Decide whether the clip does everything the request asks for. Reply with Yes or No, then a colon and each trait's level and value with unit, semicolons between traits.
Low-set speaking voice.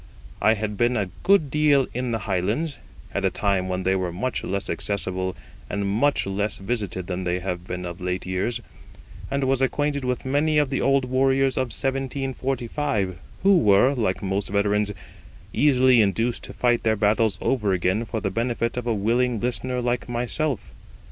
Yes: low, 115 Hz